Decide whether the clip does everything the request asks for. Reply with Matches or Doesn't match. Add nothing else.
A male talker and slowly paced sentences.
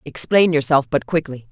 Doesn't match